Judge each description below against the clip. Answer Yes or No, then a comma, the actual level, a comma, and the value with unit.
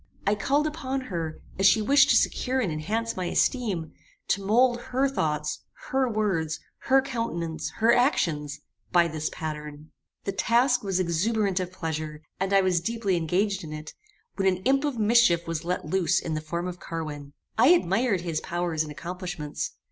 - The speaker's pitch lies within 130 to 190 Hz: Yes, medium, 185 Hz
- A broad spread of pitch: Yes, wide, 6.3 semitones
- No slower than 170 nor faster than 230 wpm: Yes, average, 175 wpm